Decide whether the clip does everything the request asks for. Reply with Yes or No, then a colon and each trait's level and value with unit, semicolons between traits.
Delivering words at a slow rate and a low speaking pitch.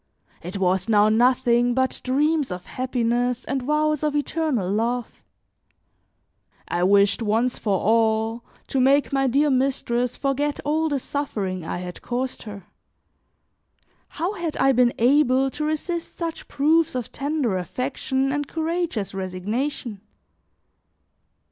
No: slow, 130 wpm; very high, 255 Hz